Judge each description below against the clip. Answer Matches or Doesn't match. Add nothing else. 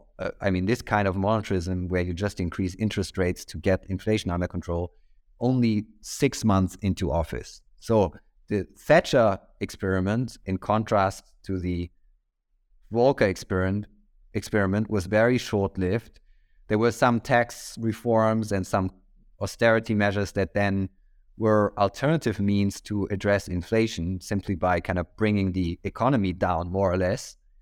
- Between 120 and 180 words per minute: Matches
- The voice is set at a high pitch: Doesn't match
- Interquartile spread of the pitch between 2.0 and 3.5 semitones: Matches